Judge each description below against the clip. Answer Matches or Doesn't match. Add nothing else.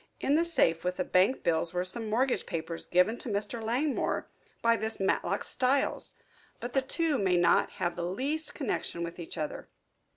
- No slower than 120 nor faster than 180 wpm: Matches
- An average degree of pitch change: Doesn't match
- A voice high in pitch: Matches